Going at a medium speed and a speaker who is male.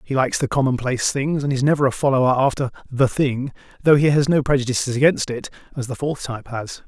No: fast, 220 wpm; male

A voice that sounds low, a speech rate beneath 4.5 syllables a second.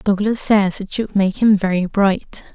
No: high, 200 Hz; 4.1 syllables/s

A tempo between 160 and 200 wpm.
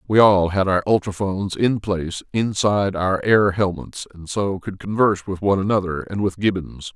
Yes: average, 180 wpm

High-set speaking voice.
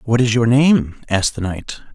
No: low, 115 Hz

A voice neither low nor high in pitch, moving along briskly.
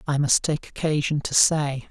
No: medium, 145 Hz; average, 190 wpm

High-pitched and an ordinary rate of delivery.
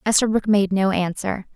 Yes: high, 195 Hz; average, 155 wpm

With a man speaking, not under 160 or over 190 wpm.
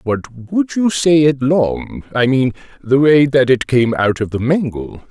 No: male; average, 200 wpm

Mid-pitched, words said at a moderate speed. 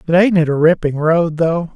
No: medium, 165 Hz; fast, 240 wpm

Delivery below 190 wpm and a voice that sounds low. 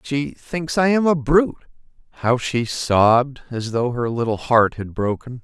Yes: average, 165 wpm; low, 130 Hz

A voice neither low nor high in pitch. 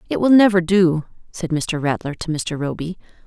Yes: medium, 170 Hz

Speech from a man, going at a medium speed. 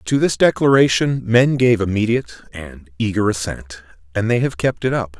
Yes: male; average, 175 wpm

